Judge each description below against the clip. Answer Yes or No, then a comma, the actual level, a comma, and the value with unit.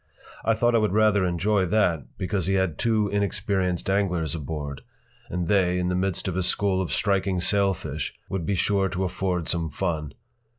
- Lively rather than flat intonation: No, average, 2.7 semitones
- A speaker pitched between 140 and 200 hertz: No, very low, 95 Hz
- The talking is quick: No, average, 180 wpm